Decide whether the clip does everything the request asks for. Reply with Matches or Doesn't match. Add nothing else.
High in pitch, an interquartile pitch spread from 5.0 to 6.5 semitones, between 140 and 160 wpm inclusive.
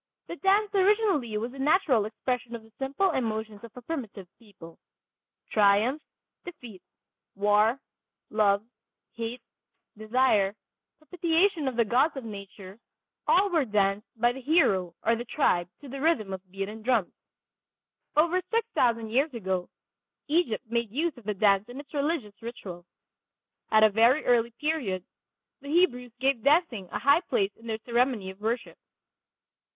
Matches